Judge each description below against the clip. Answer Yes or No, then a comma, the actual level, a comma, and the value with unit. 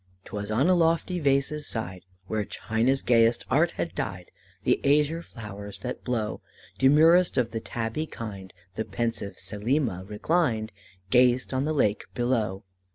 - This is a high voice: No, low, 120 Hz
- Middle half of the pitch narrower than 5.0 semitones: No, wide, 5.4 semitones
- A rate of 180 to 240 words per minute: No, average, 145 wpm